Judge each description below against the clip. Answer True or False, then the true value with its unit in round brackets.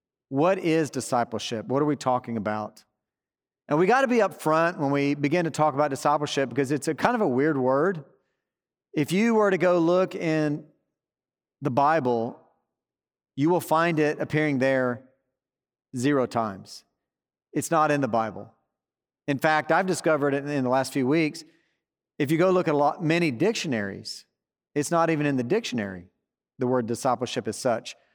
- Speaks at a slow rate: False (175 wpm)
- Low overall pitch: False (145 Hz)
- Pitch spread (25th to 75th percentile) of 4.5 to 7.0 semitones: False (3.9 semitones)